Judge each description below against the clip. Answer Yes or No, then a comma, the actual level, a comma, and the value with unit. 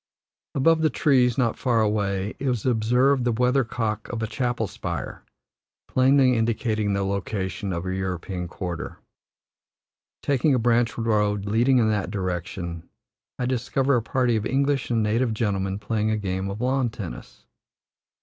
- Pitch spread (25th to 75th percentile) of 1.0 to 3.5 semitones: No, average, 4.1 semitones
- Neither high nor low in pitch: No, low, 110 Hz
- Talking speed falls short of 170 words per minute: Yes, average, 150 wpm